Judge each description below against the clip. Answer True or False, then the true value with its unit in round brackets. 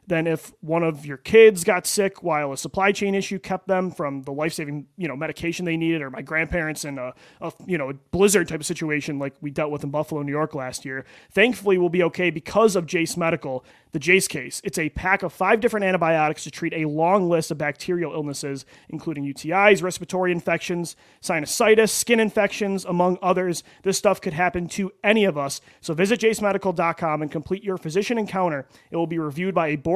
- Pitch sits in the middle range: True (170 Hz)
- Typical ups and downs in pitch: True (3.8 semitones)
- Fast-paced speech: True (210 wpm)